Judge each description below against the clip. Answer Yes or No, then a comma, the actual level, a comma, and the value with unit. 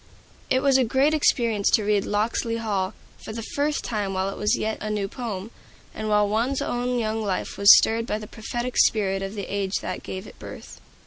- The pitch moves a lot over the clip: No, average, 2.9 semitones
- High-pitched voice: Yes, high, 215 Hz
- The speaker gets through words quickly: Yes, fast, 210 wpm